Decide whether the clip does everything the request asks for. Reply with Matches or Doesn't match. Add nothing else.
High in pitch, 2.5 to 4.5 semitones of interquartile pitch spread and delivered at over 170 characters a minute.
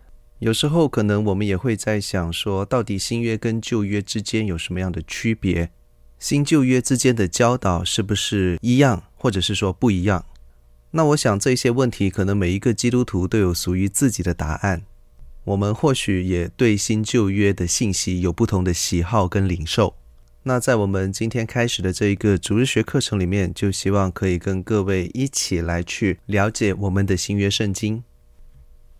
Doesn't match